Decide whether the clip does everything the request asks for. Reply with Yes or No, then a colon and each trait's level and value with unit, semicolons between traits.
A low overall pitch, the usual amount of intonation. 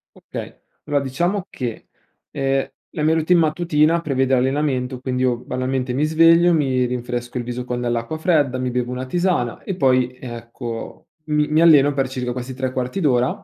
Yes: low, 130 Hz; average, 3.5 semitones